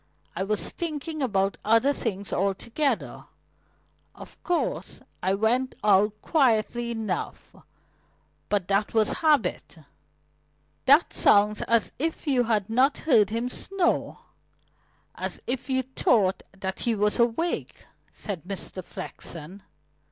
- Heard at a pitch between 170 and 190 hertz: No, high, 225 Hz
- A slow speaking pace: Yes, slow, 115 wpm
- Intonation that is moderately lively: Yes, average, 4.8 semitones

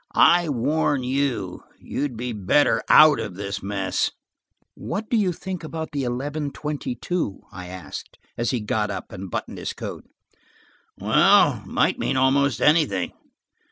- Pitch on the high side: No, low, 130 Hz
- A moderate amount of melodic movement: No, wide, 6.7 semitones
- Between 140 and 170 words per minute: Yes, average, 150 wpm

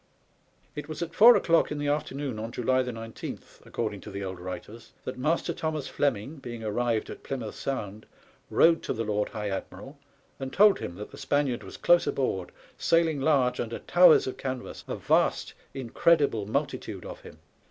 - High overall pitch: No, low, 130 Hz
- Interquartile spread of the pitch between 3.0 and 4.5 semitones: No, wide, 5.5 semitones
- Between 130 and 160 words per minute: No, average, 175 wpm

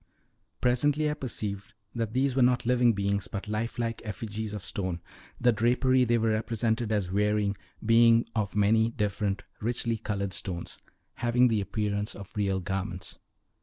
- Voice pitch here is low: Yes, low, 110 Hz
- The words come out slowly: No, average, 155 wpm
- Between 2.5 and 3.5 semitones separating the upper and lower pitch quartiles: Yes, average, 2.8 semitones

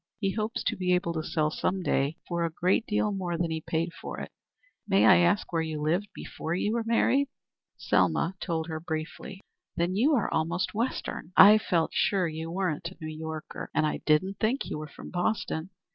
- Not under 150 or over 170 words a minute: No, fast, 205 wpm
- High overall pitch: No, medium, 175 Hz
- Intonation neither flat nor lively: Yes, average, 3.7 semitones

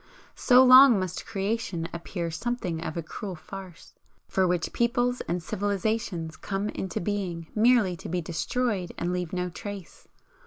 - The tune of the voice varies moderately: Yes, average, 4.3 semitones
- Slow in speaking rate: No, average, 150 wpm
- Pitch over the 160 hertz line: Yes, high, 190 Hz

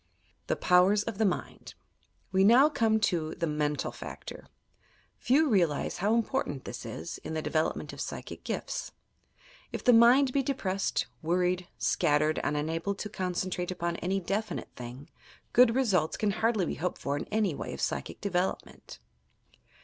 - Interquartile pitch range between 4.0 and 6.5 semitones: Yes, average, 5.1 semitones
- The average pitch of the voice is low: No, medium, 185 Hz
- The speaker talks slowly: No, average, 155 wpm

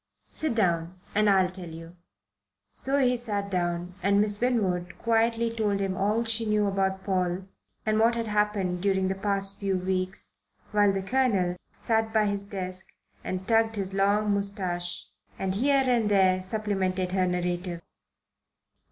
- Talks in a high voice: Yes, high, 195 Hz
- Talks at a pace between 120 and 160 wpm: Yes, average, 155 wpm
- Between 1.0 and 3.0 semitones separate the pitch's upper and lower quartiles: Yes, average, 2.7 semitones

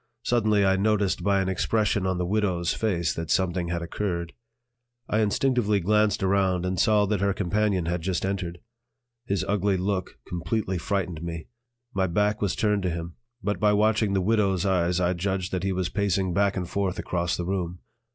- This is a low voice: Yes, very low, 95 Hz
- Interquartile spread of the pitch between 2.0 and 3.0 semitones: Yes, narrow, 2.6 semitones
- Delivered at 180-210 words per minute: Yes, average, 185 wpm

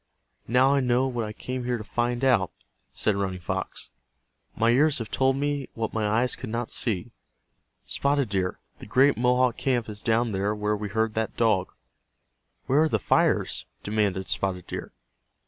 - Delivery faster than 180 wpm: No, average, 175 wpm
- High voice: No, low, 115 Hz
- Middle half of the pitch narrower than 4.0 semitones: Yes, average, 3.5 semitones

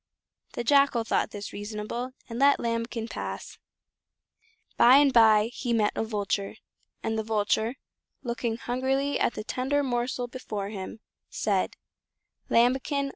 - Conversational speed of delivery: No, slow, 130 wpm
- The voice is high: Yes, high, 235 Hz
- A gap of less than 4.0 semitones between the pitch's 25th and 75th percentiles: Yes, average, 2.9 semitones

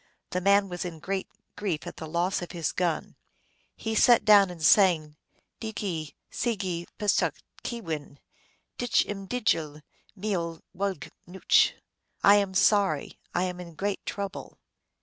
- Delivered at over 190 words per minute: No, average, 150 wpm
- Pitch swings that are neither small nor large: Yes, average, 3.3 semitones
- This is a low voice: No, medium, 185 Hz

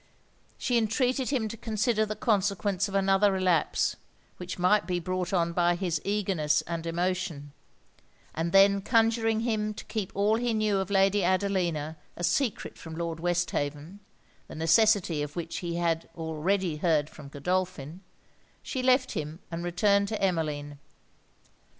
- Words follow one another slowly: No, average, 150 wpm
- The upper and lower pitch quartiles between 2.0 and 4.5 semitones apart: Yes, average, 4.0 semitones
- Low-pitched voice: No, medium, 185 Hz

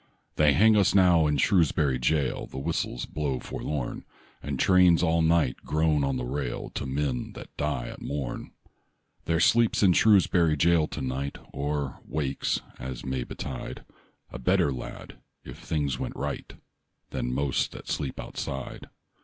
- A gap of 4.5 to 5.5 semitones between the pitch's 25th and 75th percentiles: No, average, 3.9 semitones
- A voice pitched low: Yes, very low, 75 Hz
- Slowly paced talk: No, average, 155 wpm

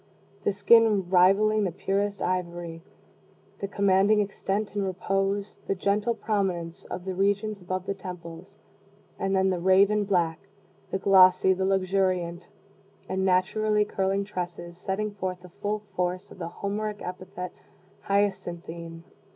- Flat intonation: Yes, narrow, 1.9 semitones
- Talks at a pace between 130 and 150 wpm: Yes, slow, 135 wpm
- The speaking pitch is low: No, high, 190 Hz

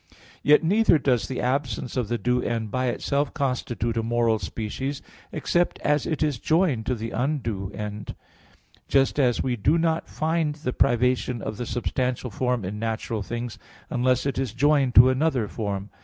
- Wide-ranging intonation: No, average, 3.8 semitones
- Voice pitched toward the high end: No, low, 125 Hz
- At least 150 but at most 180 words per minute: Yes, average, 170 wpm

